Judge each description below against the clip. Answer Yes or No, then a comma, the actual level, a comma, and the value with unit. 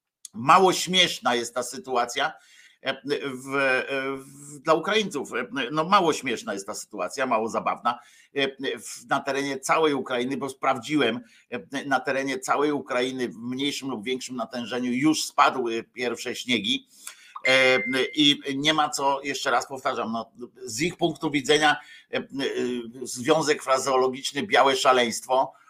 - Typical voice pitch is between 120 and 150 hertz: Yes, low, 135 Hz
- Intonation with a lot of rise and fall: No, average, 3.4 semitones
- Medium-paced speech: Yes, average, 120 wpm